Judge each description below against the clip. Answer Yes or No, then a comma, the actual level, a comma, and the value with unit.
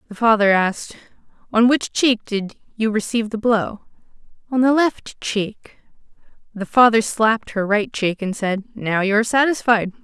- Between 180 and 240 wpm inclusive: No, average, 160 wpm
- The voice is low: No, high, 220 Hz